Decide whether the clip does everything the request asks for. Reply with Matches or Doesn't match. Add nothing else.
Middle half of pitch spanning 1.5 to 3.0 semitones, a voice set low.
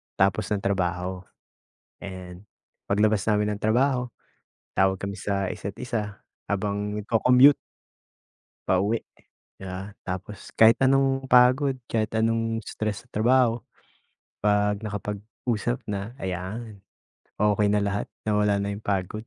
Matches